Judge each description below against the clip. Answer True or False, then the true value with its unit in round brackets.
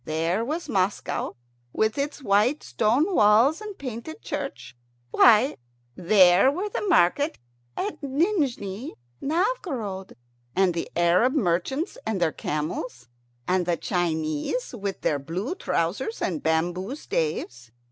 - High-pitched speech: True (205 Hz)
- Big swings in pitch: True (8.6 semitones)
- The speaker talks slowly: True (120 wpm)